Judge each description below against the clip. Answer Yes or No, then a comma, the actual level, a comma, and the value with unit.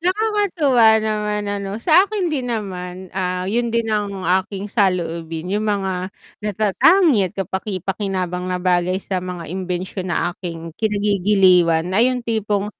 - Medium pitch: No, high, 195 Hz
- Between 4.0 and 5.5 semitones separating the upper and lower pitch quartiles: No, average, 3.2 semitones